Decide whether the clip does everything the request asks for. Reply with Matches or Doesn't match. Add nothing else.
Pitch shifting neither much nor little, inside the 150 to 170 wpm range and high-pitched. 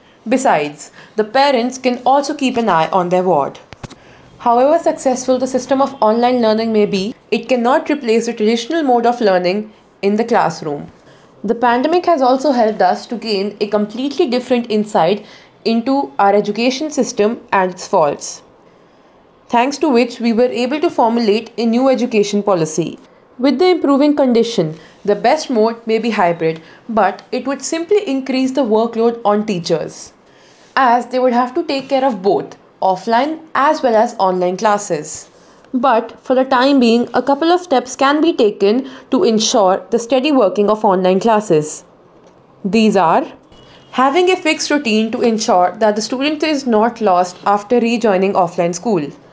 Matches